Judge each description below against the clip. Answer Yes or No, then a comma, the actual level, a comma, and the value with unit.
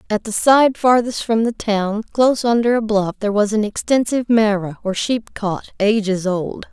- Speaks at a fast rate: No, average, 180 wpm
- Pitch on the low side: No, high, 215 Hz